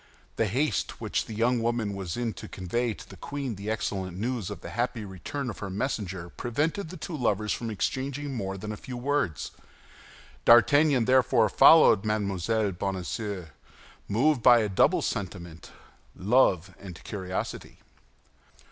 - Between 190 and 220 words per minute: No, average, 145 wpm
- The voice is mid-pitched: No, low, 110 Hz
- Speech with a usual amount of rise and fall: Yes, average, 4.5 semitones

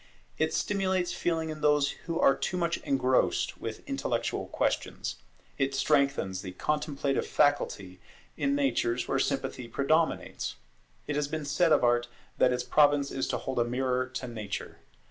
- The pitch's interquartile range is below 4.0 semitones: Yes, average, 3.3 semitones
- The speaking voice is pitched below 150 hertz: Yes, medium, 140 Hz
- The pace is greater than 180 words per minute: No, average, 155 wpm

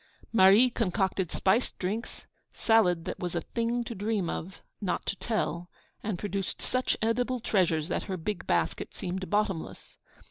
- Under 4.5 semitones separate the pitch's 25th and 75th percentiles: Yes, average, 4.0 semitones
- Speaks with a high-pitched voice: Yes, high, 195 Hz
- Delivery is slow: No, average, 150 wpm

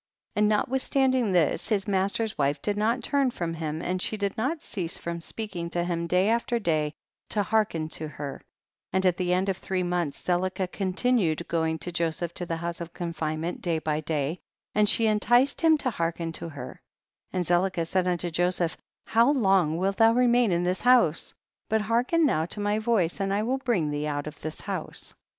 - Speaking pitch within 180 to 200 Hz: Yes, medium, 185 Hz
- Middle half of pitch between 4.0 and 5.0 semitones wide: Yes, average, 4.6 semitones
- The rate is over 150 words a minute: Yes, average, 200 wpm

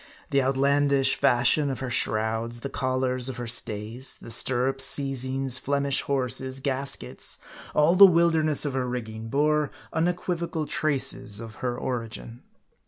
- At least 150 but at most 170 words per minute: No, slow, 135 wpm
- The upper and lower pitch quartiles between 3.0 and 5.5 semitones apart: No, narrow, 2.6 semitones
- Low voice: Yes, low, 130 Hz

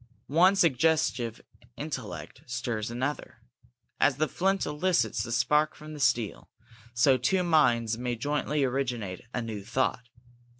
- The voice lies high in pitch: No, low, 130 Hz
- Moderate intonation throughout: Yes, average, 4.5 semitones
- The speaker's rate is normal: No, slow, 130 wpm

